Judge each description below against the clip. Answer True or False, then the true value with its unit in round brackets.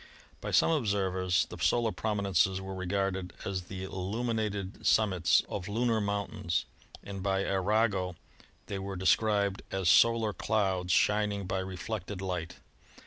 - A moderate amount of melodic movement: False (2.1 semitones)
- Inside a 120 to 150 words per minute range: True (140 wpm)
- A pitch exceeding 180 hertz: False (100 Hz)